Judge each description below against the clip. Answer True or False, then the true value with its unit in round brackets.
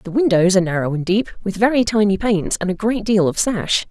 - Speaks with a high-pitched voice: True (200 Hz)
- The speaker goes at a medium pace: False (245 wpm)